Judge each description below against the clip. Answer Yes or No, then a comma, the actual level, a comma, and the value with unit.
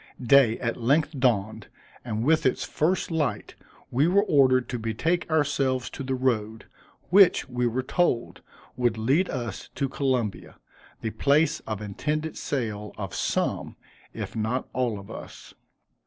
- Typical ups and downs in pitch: Yes, average, 4.6 semitones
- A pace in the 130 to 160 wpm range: Yes, average, 145 wpm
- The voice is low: Yes, low, 130 Hz